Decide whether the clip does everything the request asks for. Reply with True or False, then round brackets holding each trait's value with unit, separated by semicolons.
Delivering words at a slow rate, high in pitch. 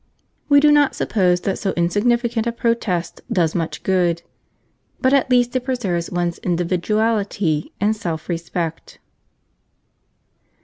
True (125 wpm; 195 Hz)